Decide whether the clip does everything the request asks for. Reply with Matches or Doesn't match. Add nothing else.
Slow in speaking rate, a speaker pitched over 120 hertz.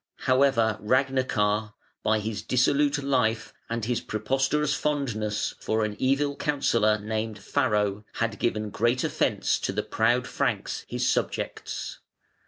Doesn't match